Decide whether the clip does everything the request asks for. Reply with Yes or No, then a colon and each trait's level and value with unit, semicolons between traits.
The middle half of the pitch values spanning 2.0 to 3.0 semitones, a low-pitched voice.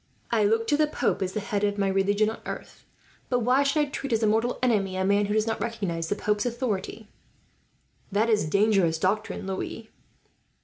No: narrow, 2.6 semitones; high, 210 Hz